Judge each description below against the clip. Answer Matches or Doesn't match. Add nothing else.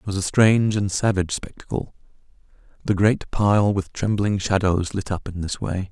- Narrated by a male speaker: Matches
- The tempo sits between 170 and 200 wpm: Matches